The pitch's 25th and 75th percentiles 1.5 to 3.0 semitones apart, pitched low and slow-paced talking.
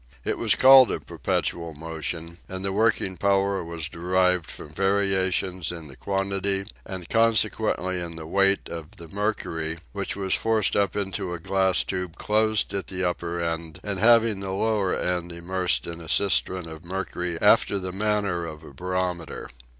No: average, 2.7 semitones; very low, 95 Hz; average, 165 wpm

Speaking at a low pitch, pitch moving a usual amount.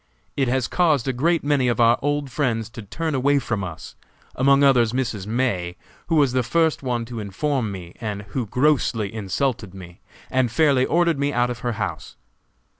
Yes: low, 125 Hz; average, 4.3 semitones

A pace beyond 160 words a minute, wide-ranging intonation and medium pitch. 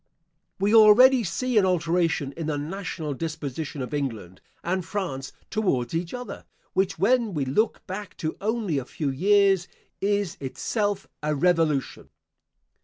No: average, 140 wpm; wide, 5.7 semitones; medium, 175 Hz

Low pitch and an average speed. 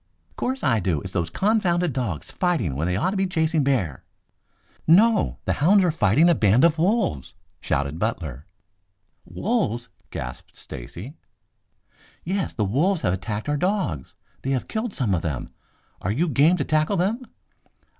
No: medium, 145 Hz; average, 160 wpm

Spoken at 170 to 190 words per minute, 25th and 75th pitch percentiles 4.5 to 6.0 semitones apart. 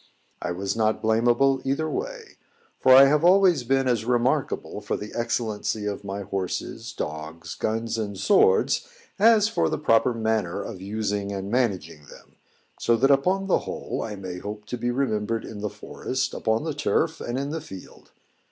Yes: average, 175 wpm; average, 5.1 semitones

